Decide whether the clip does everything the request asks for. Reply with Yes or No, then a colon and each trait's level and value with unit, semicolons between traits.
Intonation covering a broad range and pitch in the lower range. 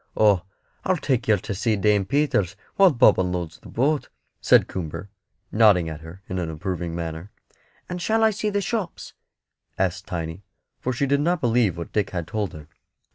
Yes: wide, 8.0 semitones; low, 100 Hz